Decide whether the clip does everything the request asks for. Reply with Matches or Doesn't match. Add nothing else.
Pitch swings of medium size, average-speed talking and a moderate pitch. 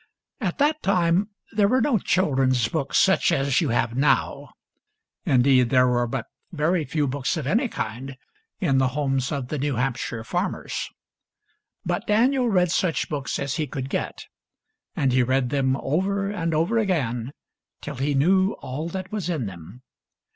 Doesn't match